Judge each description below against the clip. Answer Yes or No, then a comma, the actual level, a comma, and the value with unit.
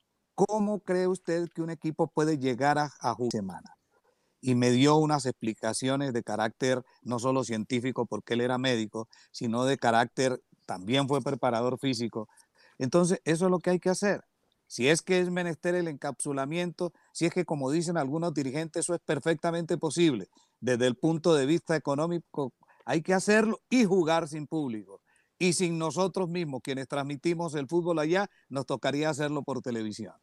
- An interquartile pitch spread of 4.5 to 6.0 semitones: Yes, average, 5.1 semitones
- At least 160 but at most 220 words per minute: Yes, average, 170 wpm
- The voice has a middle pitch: Yes, medium, 150 Hz